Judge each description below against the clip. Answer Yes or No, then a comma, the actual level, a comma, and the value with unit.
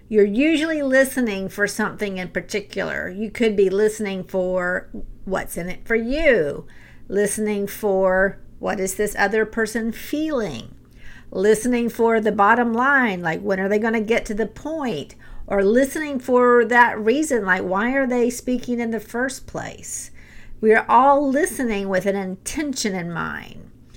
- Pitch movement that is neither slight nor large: Yes, average, 3.7 semitones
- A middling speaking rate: Yes, average, 160 wpm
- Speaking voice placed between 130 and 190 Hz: No, high, 220 Hz